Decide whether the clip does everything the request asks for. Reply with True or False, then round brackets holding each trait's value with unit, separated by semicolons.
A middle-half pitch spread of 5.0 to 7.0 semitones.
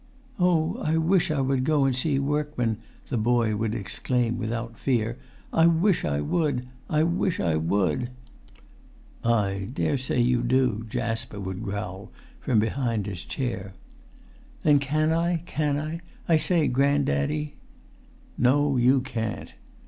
True (5.3 semitones)